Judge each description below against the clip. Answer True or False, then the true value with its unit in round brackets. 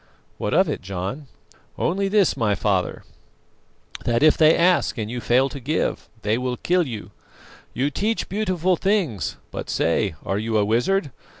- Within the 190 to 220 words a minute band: False (165 wpm)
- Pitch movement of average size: False (8.7 semitones)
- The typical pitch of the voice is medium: False (130 Hz)